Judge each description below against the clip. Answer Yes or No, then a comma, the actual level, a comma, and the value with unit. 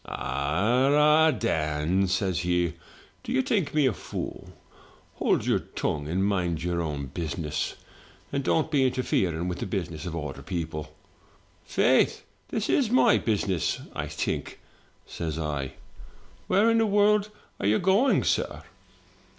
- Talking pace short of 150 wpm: Yes, average, 140 wpm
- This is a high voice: No, very low, 95 Hz